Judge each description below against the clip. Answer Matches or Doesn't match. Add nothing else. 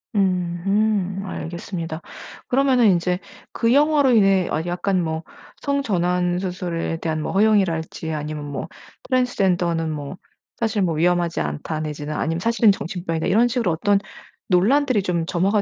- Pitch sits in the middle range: Matches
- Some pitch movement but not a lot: Matches